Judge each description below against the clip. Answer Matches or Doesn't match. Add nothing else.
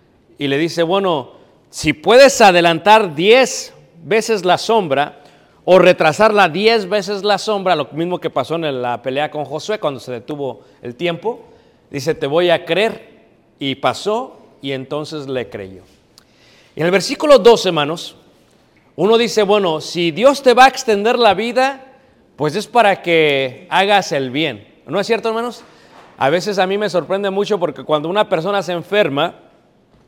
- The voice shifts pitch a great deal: Matches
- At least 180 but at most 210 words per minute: Doesn't match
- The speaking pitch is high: Doesn't match